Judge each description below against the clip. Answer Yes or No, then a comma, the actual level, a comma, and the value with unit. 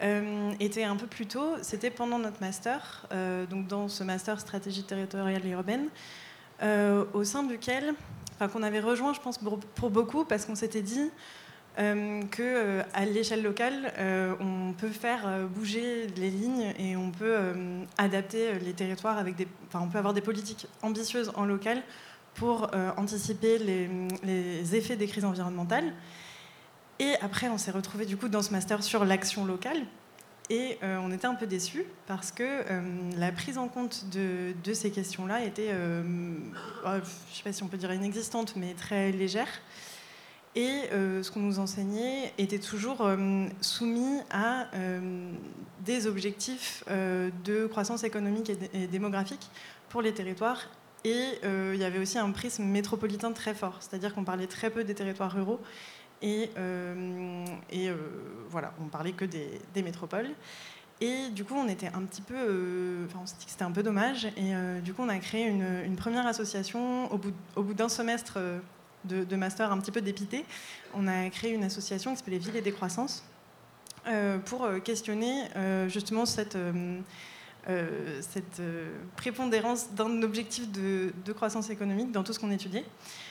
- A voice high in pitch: Yes, high, 205 Hz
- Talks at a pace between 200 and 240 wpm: No, average, 180 wpm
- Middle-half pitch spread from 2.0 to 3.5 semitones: Yes, average, 3.1 semitones